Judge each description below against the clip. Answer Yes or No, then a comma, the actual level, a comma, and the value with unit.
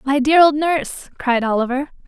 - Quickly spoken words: No, average, 175 wpm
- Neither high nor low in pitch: No, very high, 280 Hz